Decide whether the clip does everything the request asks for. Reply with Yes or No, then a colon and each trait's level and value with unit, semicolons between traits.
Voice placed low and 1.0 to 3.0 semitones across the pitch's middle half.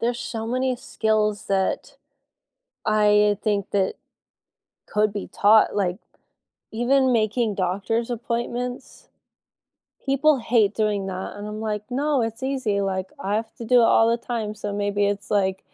No: high, 215 Hz; average, 2.7 semitones